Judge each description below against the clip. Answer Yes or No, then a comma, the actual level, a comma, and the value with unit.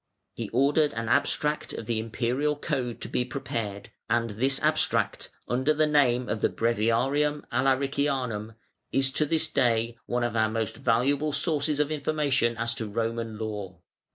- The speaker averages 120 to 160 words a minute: Yes, average, 155 wpm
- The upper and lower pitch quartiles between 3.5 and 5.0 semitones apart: Yes, average, 3.9 semitones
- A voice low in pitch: Yes, low, 125 Hz